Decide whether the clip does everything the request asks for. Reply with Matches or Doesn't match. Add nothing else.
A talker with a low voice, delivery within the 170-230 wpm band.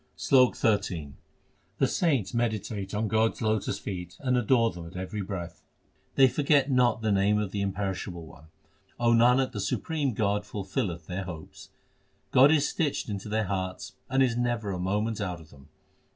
Matches